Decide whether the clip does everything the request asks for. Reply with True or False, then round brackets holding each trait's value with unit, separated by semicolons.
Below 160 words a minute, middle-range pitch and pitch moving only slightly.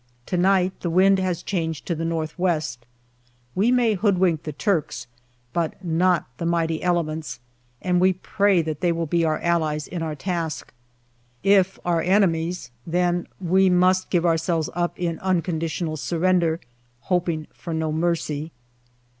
True (150 wpm; 170 Hz; 2.3 semitones)